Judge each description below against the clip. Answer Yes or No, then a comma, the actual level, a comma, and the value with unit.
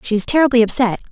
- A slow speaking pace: No, fast, 215 wpm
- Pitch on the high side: Yes, high, 235 Hz